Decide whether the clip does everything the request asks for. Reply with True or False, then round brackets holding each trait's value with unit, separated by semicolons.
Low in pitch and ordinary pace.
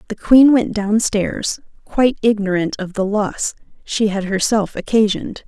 False (210 Hz; 155 wpm)